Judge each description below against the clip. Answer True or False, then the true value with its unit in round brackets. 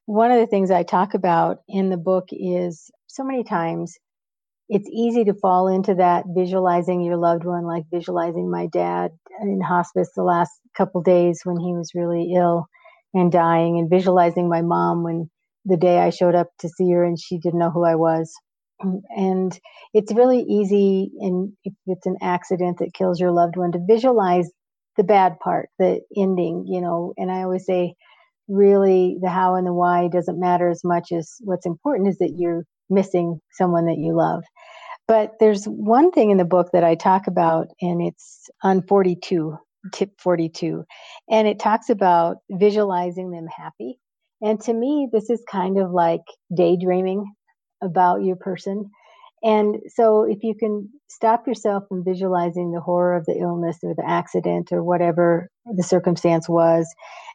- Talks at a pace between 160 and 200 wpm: True (175 wpm)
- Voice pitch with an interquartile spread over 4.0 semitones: False (2.7 semitones)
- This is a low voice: False (180 Hz)